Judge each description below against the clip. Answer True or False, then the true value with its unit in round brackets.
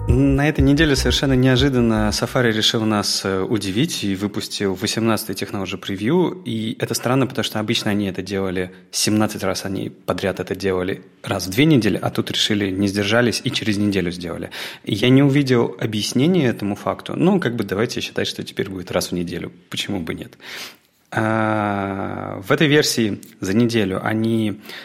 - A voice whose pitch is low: True (105 Hz)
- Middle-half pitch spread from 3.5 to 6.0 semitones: True (3.9 semitones)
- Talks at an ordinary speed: False (165 wpm)